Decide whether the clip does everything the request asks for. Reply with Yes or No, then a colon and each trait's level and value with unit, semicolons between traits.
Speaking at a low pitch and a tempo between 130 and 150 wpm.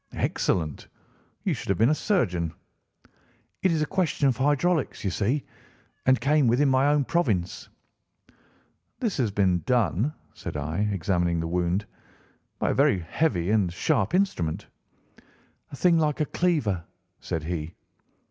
Yes: low, 110 Hz; average, 145 wpm